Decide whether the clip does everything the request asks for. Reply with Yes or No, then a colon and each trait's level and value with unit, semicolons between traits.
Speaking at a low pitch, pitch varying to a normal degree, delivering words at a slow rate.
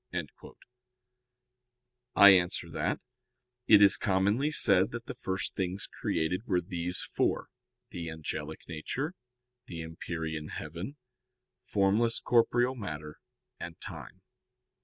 Yes: very low, 95 Hz; average, 4.6 semitones; slow, 105 wpm